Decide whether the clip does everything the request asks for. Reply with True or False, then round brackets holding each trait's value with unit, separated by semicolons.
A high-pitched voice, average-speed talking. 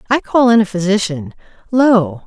True (205 Hz; 160 wpm)